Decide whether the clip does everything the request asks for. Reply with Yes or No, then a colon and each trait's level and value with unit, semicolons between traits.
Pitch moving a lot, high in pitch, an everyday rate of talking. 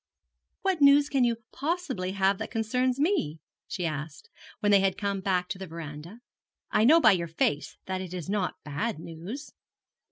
Yes: wide, 6.7 semitones; high, 195 Hz; average, 180 wpm